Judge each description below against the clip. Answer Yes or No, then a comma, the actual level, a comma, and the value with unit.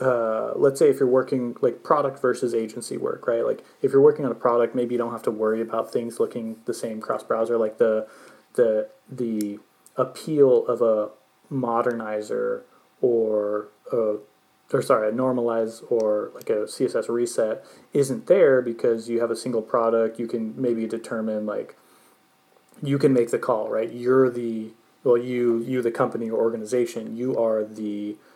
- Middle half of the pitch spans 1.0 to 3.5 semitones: Yes, average, 3.2 semitones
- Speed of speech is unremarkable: Yes, average, 170 wpm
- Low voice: Yes, low, 120 Hz